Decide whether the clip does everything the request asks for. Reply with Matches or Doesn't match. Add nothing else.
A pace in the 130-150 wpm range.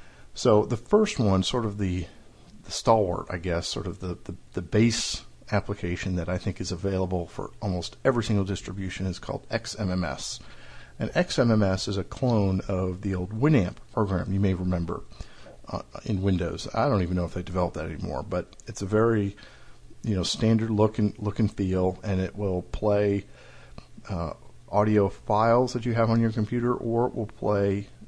Doesn't match